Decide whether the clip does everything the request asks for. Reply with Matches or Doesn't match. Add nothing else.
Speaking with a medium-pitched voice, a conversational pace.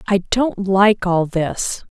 Doesn't match